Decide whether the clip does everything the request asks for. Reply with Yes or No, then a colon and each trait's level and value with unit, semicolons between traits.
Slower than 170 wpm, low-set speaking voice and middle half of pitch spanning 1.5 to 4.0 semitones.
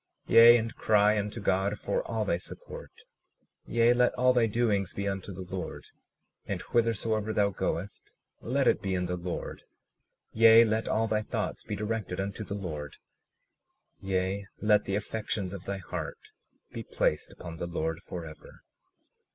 Yes: average, 160 wpm; low, 100 Hz; average, 3.4 semitones